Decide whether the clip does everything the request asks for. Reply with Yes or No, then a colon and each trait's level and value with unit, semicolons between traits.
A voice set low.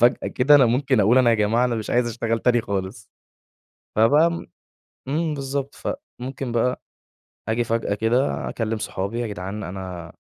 Yes: low, 115 Hz